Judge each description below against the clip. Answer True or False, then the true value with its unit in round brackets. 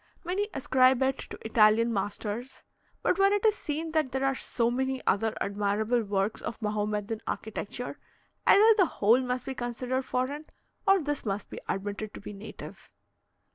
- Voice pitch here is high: True (245 Hz)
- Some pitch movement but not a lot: True (4.2 semitones)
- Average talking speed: True (165 wpm)